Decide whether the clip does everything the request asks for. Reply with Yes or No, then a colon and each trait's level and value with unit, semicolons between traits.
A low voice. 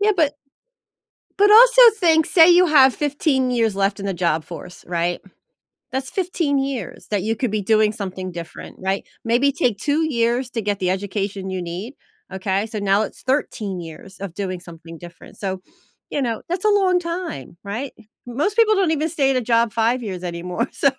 No: high, 225 Hz